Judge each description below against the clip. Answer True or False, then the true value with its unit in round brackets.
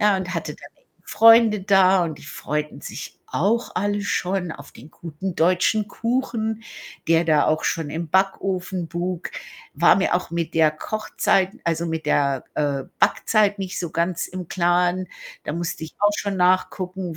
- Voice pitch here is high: False (180 Hz)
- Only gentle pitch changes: False (3.1 semitones)